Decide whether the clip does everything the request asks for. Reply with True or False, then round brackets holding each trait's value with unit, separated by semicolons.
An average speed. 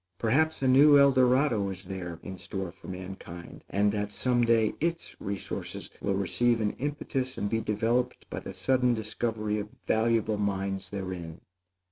True (160 wpm)